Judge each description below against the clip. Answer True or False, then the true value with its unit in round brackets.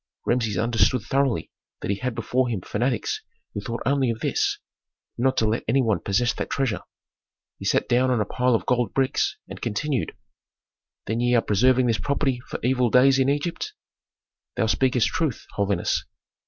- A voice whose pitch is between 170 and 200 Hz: False (120 Hz)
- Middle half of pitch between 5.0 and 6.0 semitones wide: False (2.8 semitones)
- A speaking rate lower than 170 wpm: False (175 wpm)